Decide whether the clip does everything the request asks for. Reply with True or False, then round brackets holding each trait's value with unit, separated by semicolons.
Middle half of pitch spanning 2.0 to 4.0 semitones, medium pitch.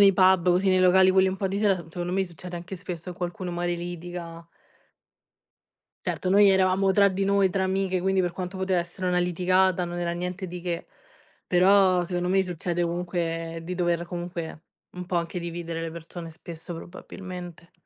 False (1.5 semitones; 180 Hz)